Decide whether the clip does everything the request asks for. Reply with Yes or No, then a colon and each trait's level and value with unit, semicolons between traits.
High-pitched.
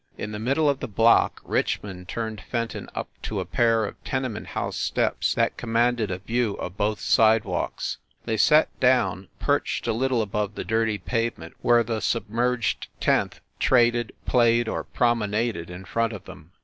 No: low, 115 Hz